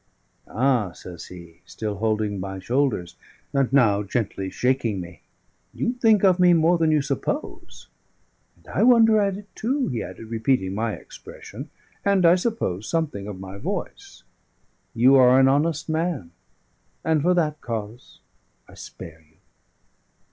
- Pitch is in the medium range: No, low, 130 Hz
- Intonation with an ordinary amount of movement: No, wide, 8.8 semitones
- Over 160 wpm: No, average, 150 wpm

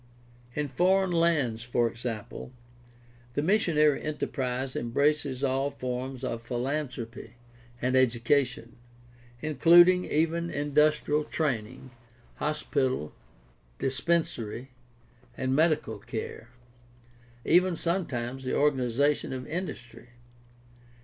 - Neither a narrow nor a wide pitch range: Yes, average, 3.7 semitones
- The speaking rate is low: Yes, slow, 90 wpm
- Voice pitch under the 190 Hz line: Yes, low, 135 Hz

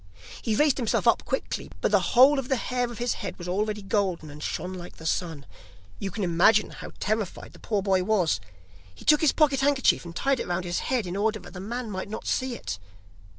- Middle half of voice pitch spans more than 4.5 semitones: Yes, wide, 5.4 semitones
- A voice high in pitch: Yes, high, 210 Hz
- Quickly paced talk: Yes, fast, 230 wpm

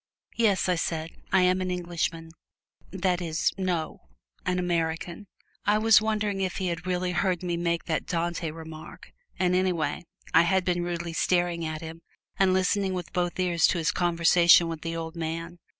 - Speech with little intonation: Yes, narrow, 1.8 semitones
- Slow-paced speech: No, average, 175 wpm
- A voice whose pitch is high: No, medium, 175 Hz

